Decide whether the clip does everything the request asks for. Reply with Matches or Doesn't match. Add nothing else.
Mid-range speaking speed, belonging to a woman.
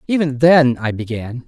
Doesn't match